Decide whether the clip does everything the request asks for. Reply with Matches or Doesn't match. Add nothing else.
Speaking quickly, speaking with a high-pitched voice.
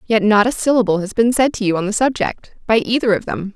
Matches